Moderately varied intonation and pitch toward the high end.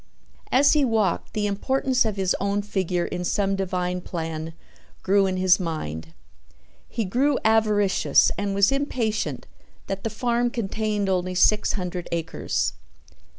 Yes: average, 3.4 semitones; high, 200 Hz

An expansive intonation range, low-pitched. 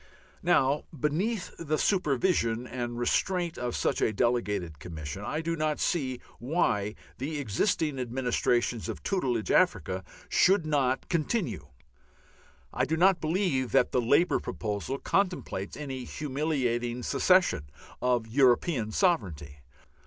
Yes: wide, 5.7 semitones; low, 130 Hz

